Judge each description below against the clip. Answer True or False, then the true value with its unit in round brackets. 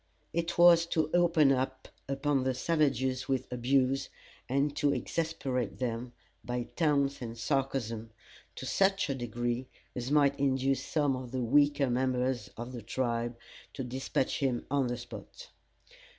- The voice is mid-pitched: False (130 Hz)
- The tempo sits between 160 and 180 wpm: False (140 wpm)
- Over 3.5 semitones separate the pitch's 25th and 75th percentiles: False (2.8 semitones)